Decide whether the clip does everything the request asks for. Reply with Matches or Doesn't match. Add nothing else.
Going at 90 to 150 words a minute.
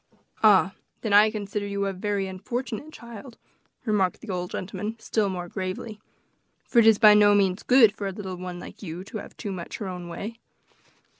Doesn't match